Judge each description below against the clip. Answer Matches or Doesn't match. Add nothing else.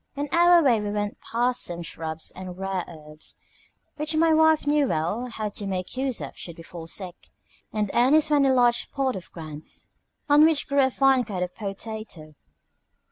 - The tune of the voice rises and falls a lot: Matches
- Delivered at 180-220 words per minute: Matches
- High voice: Matches